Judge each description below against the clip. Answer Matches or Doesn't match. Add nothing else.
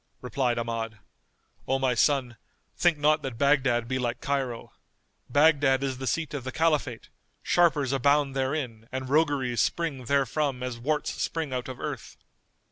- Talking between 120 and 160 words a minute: Matches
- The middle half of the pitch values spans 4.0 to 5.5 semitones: Doesn't match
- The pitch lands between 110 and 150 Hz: Matches